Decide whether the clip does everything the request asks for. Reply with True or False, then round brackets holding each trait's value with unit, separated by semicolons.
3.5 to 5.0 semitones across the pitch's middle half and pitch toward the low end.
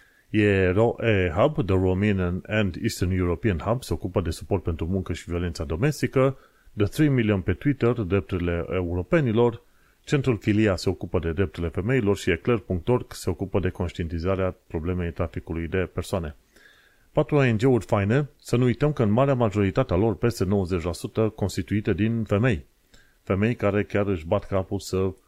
True (3.9 semitones; 100 Hz)